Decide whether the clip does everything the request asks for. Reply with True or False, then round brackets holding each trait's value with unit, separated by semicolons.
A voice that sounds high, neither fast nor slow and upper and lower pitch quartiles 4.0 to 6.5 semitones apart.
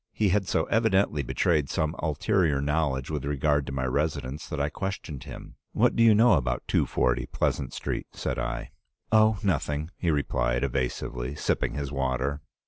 False (75 Hz; 165 wpm; 4.5 semitones)